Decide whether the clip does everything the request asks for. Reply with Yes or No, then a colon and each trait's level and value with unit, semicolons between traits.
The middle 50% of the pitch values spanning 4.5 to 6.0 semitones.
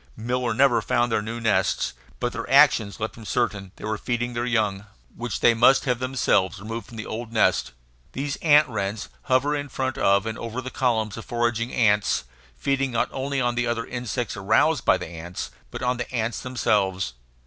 No: average, 2.7 semitones